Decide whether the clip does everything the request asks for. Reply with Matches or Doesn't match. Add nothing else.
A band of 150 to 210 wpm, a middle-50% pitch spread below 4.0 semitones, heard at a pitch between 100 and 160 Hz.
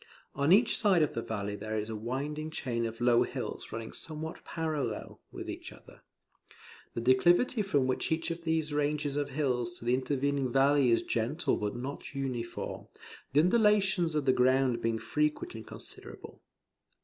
Doesn't match